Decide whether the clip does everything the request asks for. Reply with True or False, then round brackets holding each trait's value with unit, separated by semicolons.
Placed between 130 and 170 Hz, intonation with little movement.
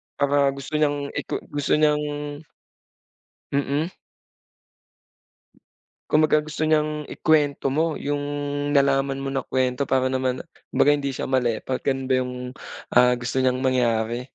True (140 Hz; 2.2 semitones)